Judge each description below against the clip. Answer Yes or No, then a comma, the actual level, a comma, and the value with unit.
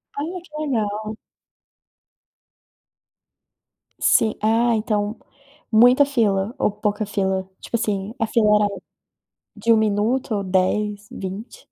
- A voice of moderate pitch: No, high, 215 Hz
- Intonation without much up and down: Yes, narrow, 2.1 semitones